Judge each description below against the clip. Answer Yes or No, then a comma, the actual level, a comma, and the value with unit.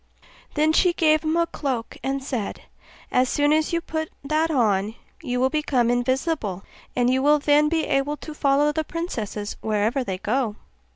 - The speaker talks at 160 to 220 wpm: Yes, average, 175 wpm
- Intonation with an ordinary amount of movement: Yes, average, 4.2 semitones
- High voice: Yes, very high, 275 Hz